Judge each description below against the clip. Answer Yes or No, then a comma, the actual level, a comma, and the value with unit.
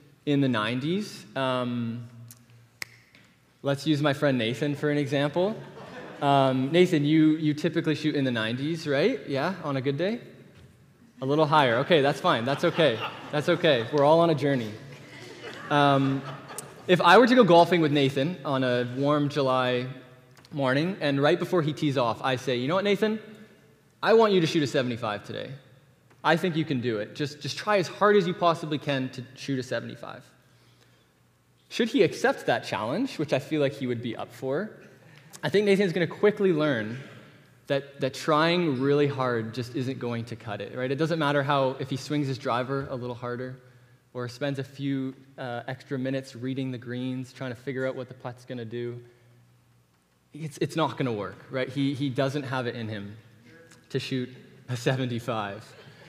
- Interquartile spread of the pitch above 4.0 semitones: No, average, 3.4 semitones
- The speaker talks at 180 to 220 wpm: Yes, average, 190 wpm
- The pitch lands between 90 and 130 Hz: No, medium, 140 Hz